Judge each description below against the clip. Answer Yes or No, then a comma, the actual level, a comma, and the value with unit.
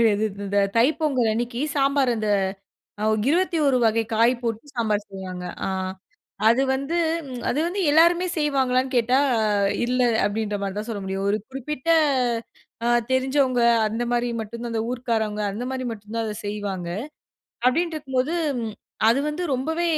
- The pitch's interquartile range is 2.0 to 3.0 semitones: No, average, 4.2 semitones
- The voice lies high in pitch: Yes, high, 245 Hz